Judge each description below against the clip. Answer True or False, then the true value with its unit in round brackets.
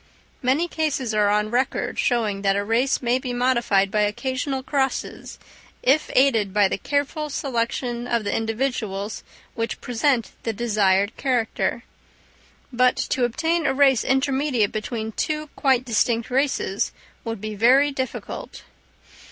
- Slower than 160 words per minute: True (135 wpm)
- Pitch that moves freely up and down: False (3.8 semitones)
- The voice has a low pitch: False (245 Hz)